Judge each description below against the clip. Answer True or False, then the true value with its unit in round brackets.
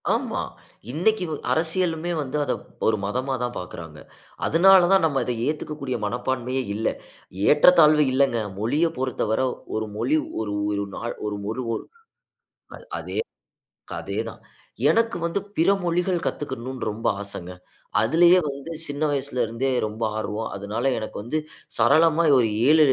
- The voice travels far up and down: True (6.2 semitones)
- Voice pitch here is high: False (135 Hz)